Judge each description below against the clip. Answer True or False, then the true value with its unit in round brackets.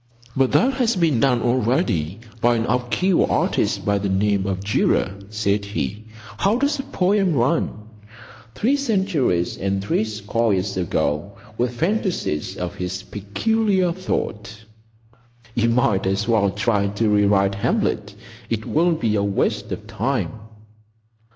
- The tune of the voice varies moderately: False (8.5 semitones)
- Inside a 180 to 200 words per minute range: False (140 wpm)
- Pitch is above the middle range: False (110 Hz)